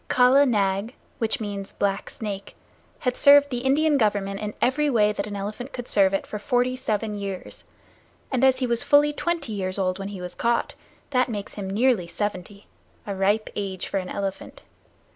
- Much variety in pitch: No, average, 4.3 semitones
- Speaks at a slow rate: No, average, 185 wpm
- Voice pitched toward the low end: No, high, 210 Hz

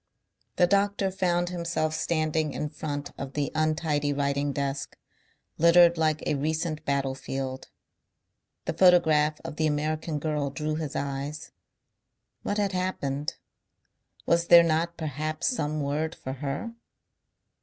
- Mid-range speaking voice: Yes, medium, 155 Hz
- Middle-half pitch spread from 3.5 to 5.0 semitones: No, average, 2.8 semitones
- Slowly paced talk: Yes, slow, 125 wpm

